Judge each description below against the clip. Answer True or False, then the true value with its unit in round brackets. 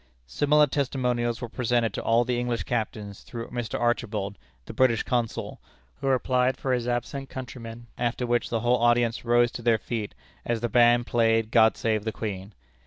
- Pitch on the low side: True (120 Hz)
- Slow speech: False (175 wpm)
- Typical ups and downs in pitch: False (1.4 semitones)